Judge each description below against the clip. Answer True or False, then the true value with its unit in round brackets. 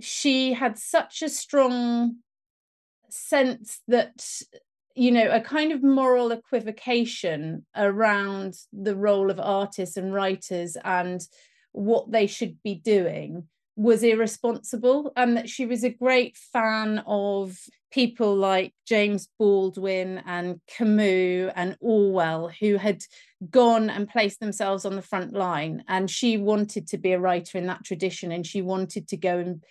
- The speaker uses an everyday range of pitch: True (3.9 semitones)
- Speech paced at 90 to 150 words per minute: True (145 wpm)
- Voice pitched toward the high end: True (210 Hz)